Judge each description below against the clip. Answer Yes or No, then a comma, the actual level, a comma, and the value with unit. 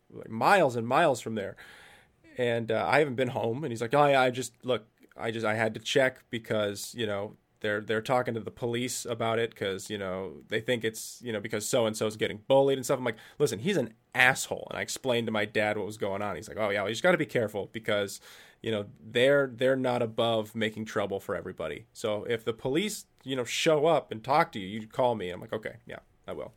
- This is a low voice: Yes, low, 115 Hz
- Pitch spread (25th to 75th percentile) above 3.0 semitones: No, narrow, 2.6 semitones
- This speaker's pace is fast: Yes, fast, 255 wpm